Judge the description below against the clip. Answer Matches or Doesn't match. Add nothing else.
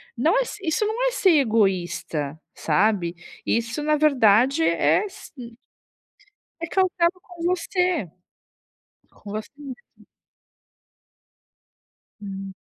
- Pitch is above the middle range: Matches